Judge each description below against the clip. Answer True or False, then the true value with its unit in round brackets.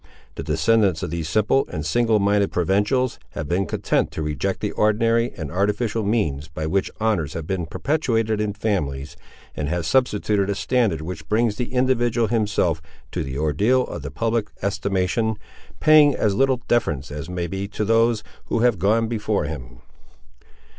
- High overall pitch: False (105 Hz)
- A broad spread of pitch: True (5.7 semitones)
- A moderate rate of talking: True (165 wpm)